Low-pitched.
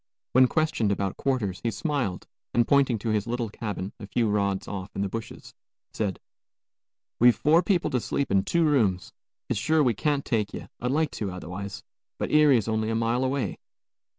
Yes: low, 115 Hz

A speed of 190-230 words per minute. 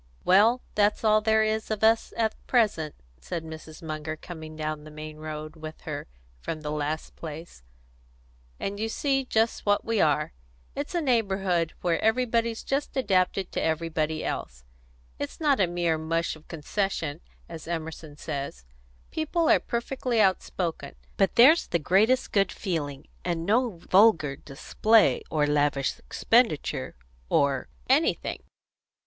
No: average, 140 wpm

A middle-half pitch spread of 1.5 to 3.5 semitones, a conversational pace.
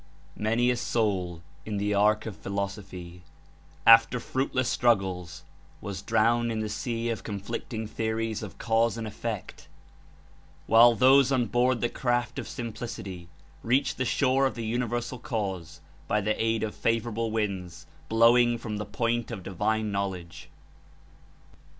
Yes: average, 2.8 semitones; average, 145 wpm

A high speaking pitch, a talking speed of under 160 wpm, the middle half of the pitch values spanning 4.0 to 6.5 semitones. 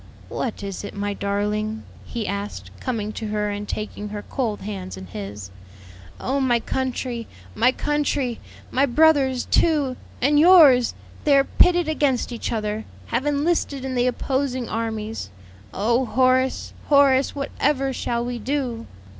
Yes: high, 245 Hz; average, 145 wpm; average, 4.4 semitones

